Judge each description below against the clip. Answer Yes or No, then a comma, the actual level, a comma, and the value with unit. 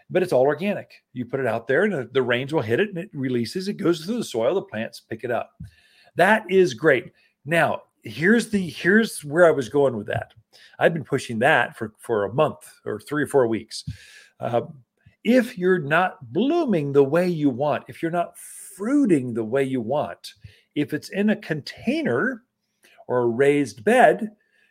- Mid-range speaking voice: Yes, medium, 155 Hz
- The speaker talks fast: No, average, 195 wpm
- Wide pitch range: Yes, wide, 6.4 semitones